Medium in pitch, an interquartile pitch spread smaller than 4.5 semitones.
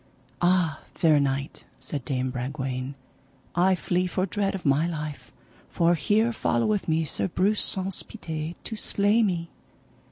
No: medium, 170 Hz; average, 5.0 semitones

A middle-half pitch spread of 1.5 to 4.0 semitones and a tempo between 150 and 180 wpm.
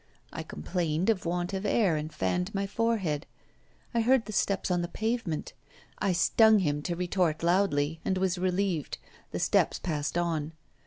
Yes: average, 3.5 semitones; average, 170 wpm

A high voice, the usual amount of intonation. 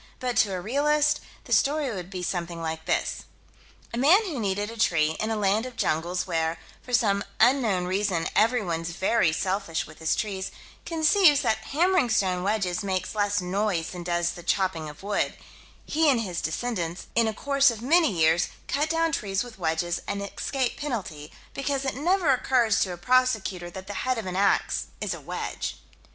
No: high, 205 Hz; wide, 6.2 semitones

